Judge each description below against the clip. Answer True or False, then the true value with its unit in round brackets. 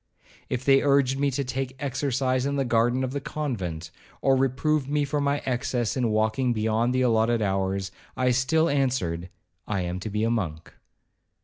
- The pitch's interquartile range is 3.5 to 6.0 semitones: True (3.9 semitones)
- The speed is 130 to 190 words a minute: True (180 wpm)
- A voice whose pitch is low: True (125 Hz)